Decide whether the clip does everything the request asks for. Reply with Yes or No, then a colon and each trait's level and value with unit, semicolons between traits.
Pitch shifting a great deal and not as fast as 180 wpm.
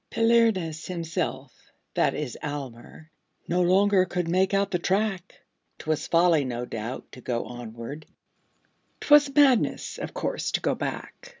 Yes: wide, 6.4 semitones; slow, 135 wpm